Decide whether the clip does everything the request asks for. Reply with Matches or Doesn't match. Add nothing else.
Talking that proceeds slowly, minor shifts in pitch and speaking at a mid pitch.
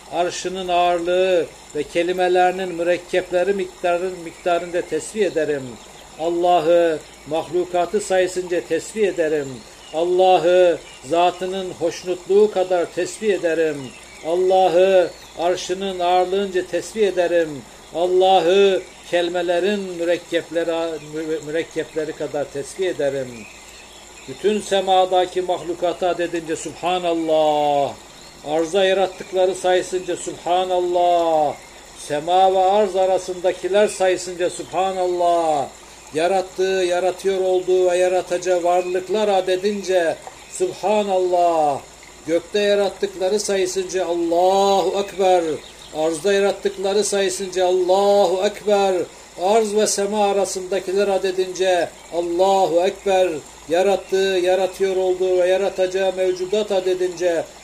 Matches